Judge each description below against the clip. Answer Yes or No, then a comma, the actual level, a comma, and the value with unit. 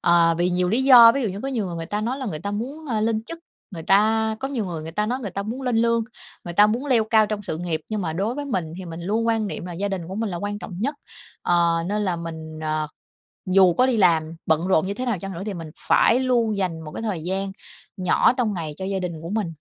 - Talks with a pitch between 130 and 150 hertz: No, high, 200 Hz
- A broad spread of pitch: No, average, 4.7 semitones